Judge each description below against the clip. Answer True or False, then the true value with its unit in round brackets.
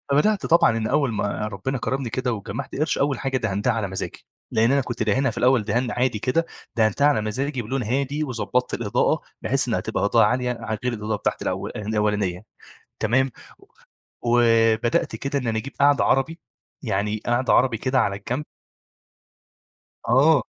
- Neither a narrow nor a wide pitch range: True (3.6 semitones)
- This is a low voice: True (120 Hz)